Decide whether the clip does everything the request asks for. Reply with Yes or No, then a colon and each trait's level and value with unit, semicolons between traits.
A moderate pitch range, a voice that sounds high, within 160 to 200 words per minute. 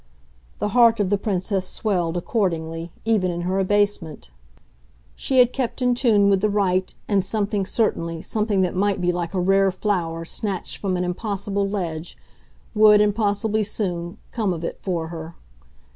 Yes: average, 3.1 semitones; high, 195 Hz; average, 165 wpm